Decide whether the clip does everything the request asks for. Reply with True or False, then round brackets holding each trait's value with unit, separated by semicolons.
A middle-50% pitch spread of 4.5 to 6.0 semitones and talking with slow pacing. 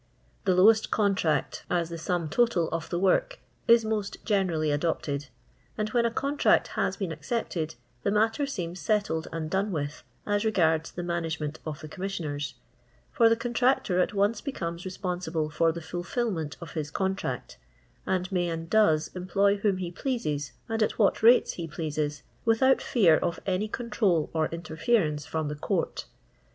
False (5.0 semitones; 165 wpm)